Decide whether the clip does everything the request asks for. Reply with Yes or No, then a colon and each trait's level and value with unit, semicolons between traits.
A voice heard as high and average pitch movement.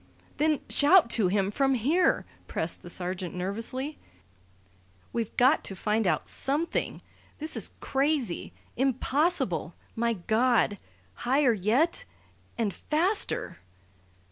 No: high, 245 Hz; wide, 6.5 semitones